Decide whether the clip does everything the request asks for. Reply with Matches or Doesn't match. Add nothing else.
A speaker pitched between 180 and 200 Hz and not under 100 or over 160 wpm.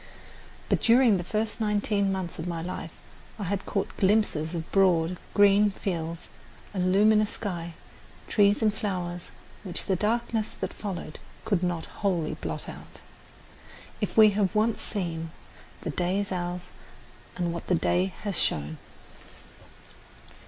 Matches